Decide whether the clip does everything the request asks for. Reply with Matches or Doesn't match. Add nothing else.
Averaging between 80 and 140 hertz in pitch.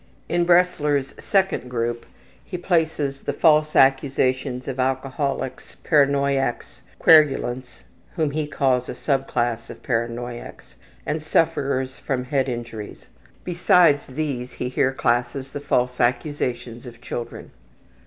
Matches